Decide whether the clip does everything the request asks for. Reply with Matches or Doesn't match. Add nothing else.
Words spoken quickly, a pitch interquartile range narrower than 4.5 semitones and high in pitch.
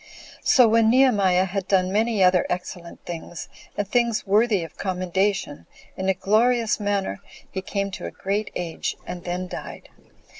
Doesn't match